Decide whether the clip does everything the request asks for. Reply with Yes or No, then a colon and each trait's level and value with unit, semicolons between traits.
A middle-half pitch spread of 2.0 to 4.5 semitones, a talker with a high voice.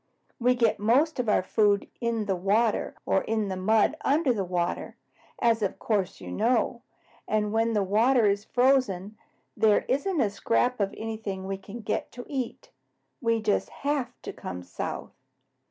Yes: average, 3.4 semitones; high, 220 Hz